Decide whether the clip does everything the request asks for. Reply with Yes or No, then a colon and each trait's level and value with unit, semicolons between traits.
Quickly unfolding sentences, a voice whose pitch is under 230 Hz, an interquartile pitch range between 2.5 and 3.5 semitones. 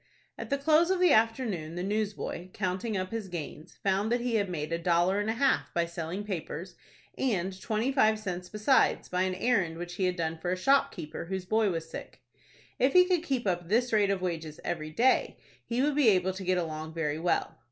No: fast, 215 wpm; high, 190 Hz; average, 4.8 semitones